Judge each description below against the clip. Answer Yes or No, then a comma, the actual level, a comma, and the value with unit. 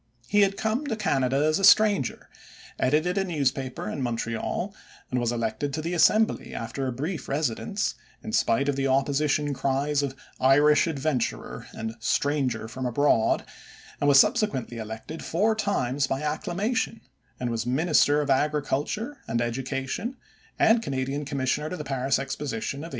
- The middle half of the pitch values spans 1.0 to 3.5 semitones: No, average, 4.6 semitones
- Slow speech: No, average, 155 wpm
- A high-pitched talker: No, medium, 140 Hz